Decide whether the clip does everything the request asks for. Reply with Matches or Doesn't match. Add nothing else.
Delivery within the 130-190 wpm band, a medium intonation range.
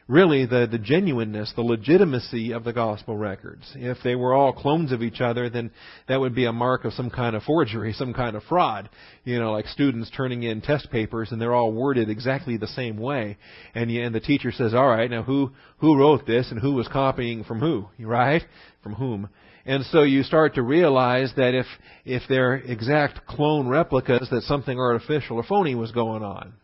Doesn't match